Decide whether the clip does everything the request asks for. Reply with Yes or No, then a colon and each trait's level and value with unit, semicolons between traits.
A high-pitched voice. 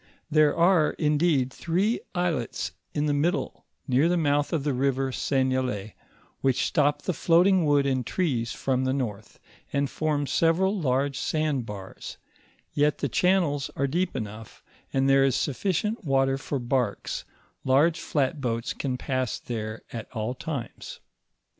No: medium, 140 Hz